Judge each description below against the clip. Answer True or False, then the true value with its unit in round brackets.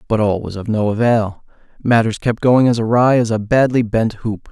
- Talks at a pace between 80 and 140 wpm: False (200 wpm)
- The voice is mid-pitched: False (115 Hz)